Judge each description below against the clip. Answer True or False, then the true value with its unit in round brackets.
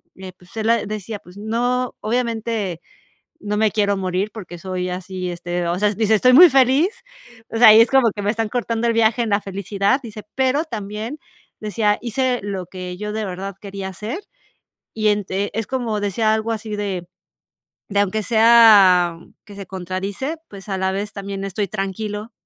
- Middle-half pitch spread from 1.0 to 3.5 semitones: True (2.9 semitones)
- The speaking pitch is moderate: False (210 Hz)